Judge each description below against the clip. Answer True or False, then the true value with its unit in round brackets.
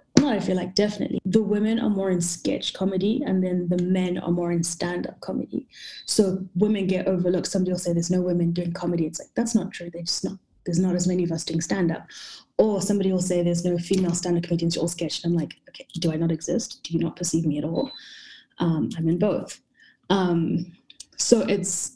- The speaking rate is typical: False (220 wpm)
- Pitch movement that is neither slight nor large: False (2.2 semitones)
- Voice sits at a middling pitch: True (180 Hz)